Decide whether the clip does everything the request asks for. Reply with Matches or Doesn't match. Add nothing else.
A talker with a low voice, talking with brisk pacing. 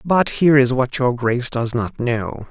Matches